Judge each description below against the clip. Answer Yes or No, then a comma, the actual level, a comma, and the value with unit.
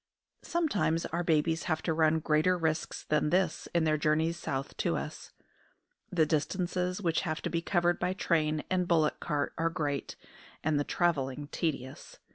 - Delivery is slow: No, average, 165 wpm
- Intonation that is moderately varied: No, narrow, 2.2 semitones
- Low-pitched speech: No, medium, 160 Hz